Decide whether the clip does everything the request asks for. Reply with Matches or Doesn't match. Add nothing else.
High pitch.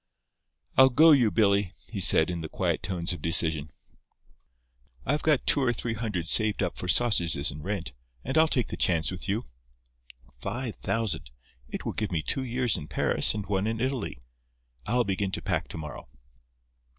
Doesn't match